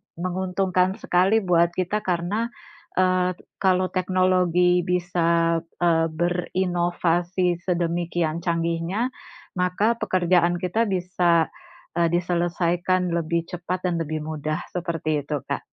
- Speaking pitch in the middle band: Yes, medium, 175 Hz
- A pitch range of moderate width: No, narrow, 1.5 semitones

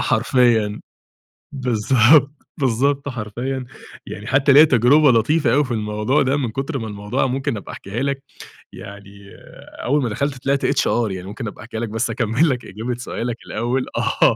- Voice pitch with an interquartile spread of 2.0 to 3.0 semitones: No, average, 3.8 semitones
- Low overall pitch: Yes, low, 125 Hz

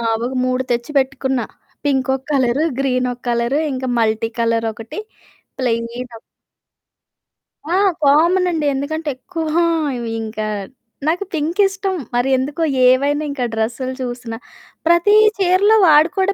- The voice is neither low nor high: No, very high, 265 Hz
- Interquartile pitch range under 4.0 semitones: No, average, 4.9 semitones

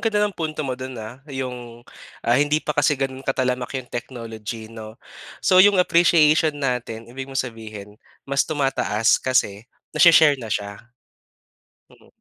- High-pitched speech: No, low, 130 Hz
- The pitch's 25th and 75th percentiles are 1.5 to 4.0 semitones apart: No, average, 4.4 semitones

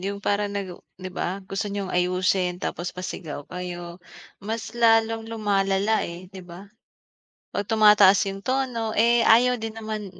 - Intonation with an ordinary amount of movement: Yes, average, 3.3 semitones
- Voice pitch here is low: No, high, 200 Hz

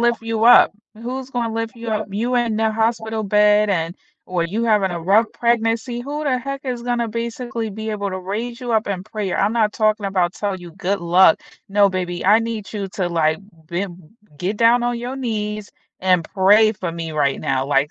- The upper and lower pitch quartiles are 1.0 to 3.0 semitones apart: No, average, 3.7 semitones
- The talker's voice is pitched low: No, high, 215 Hz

